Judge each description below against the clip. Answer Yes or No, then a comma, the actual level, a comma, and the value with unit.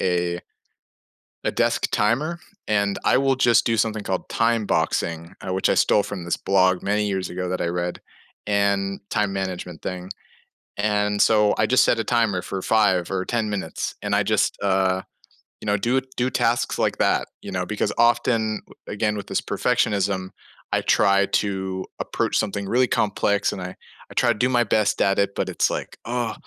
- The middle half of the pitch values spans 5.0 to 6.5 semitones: No, average, 2.9 semitones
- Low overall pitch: Yes, low, 100 Hz